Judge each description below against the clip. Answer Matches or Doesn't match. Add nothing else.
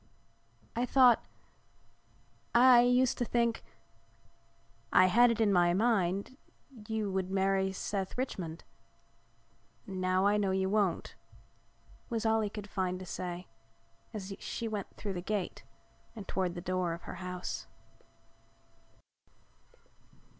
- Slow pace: Matches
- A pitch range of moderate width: Matches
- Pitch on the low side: Doesn't match